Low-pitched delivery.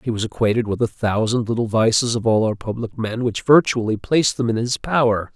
Yes: low, 115 Hz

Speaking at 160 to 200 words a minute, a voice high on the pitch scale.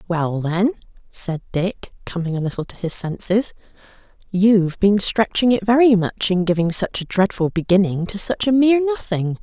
Yes: average, 170 wpm; high, 195 Hz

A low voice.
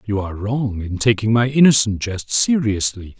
Yes: low, 110 Hz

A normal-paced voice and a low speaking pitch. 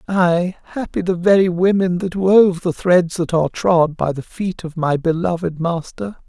No: average, 180 wpm; medium, 175 Hz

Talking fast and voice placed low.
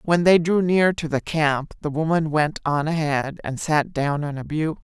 No: fast, 220 wpm; medium, 155 Hz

